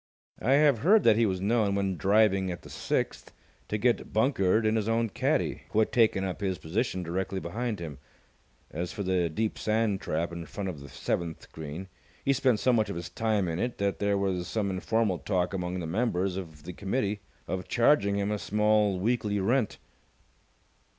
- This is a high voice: No, low, 100 Hz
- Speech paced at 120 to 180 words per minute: No, average, 195 wpm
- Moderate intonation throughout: Yes, average, 3.4 semitones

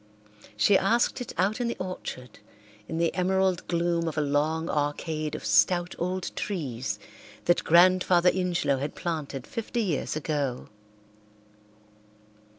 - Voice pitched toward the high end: No, medium, 170 Hz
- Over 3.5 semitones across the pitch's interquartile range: Yes, average, 4.0 semitones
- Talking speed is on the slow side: Yes, slow, 130 wpm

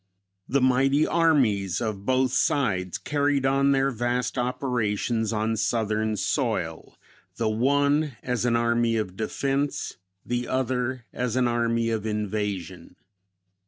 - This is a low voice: Yes, low, 120 Hz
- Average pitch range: Yes, average, 3.5 semitones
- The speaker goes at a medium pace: No, slow, 125 wpm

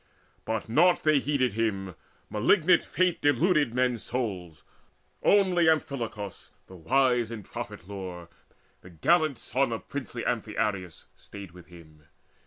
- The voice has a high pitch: No, low, 115 Hz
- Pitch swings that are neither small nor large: No, wide, 6.9 semitones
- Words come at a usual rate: No, slow, 125 wpm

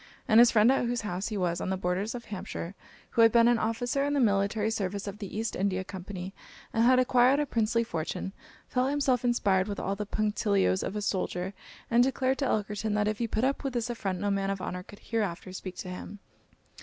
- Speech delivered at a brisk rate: Yes, fast, 230 wpm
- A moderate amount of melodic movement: Yes, average, 3.6 semitones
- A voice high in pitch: Yes, high, 210 Hz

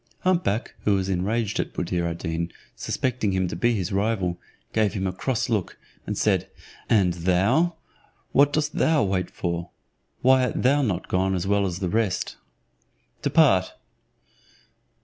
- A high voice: No, low, 100 Hz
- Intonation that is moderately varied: Yes, average, 4.8 semitones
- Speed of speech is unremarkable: Yes, average, 160 wpm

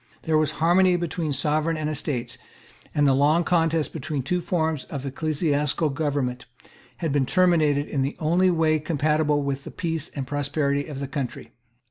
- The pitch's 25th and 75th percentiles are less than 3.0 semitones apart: Yes, narrow, 2.5 semitones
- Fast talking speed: No, average, 175 wpm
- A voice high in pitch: No, medium, 150 Hz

